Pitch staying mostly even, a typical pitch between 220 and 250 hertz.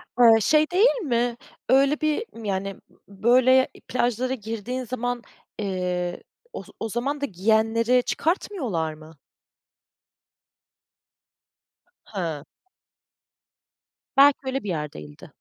No: average, 5.2 semitones; high, 235 Hz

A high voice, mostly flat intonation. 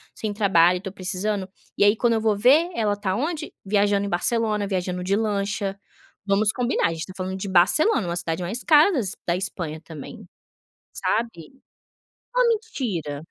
No: high, 200 Hz; average, 3.8 semitones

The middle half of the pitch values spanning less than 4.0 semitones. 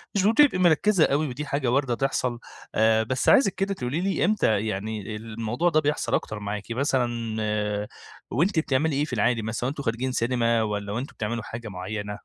No: average, 5.3 semitones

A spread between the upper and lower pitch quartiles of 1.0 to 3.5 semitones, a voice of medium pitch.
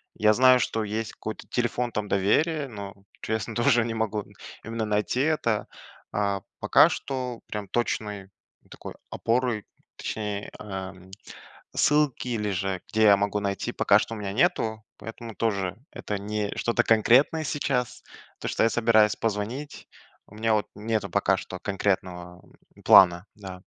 No: average, 2.7 semitones; low, 110 Hz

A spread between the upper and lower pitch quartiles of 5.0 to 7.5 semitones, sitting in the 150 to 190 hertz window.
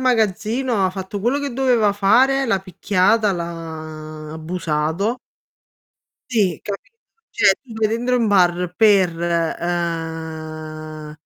Yes: wide, 5.5 semitones; medium, 185 Hz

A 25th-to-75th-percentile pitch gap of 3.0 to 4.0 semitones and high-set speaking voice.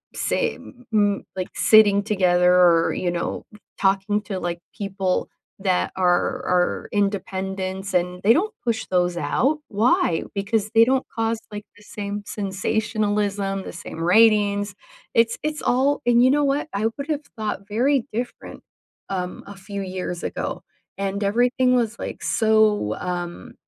Yes: average, 3.3 semitones; high, 205 Hz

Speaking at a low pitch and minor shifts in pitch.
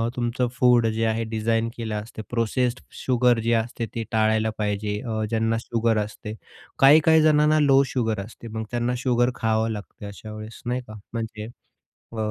Yes: low, 115 Hz; narrow, 2.0 semitones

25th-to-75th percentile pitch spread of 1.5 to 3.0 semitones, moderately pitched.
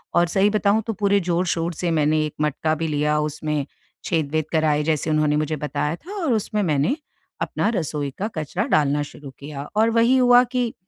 No: average, 5.1 semitones; medium, 160 Hz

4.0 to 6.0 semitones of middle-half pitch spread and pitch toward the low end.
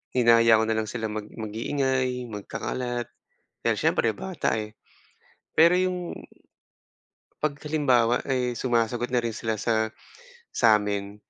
No: average, 2.7 semitones; low, 120 Hz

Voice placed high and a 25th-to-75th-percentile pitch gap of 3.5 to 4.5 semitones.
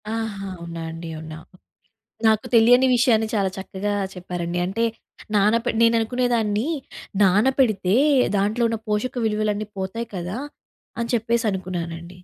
Yes: high, 210 Hz; average, 3.8 semitones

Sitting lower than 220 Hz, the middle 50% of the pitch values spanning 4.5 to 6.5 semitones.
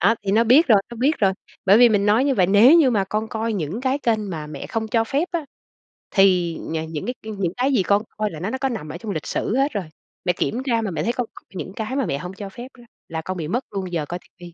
Yes: high, 210 Hz; average, 5.1 semitones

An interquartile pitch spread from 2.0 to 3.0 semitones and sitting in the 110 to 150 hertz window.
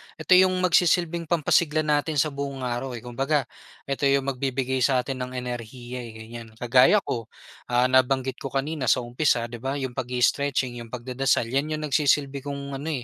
Yes: narrow, 2.6 semitones; low, 135 Hz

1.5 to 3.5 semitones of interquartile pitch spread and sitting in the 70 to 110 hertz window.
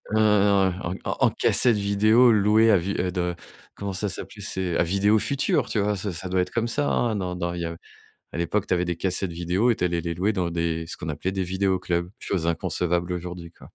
Yes: average, 2.8 semitones; very low, 95 Hz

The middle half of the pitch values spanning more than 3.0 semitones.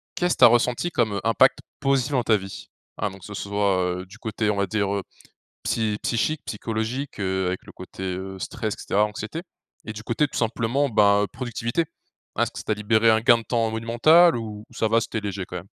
No: average, 2.7 semitones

